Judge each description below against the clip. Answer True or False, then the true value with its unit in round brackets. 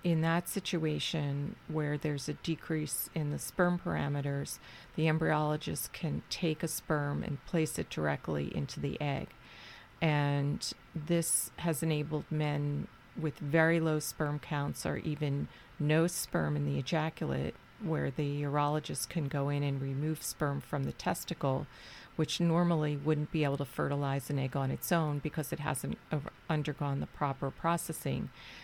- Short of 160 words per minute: True (150 wpm)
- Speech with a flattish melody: True (2.2 semitones)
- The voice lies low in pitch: False (150 Hz)